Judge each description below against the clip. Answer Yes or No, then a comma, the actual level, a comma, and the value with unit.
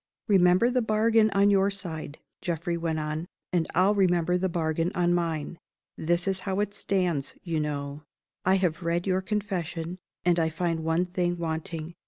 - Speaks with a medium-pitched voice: Yes, medium, 175 Hz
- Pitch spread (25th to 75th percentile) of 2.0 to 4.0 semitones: Yes, average, 2.7 semitones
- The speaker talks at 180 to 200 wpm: No, average, 170 wpm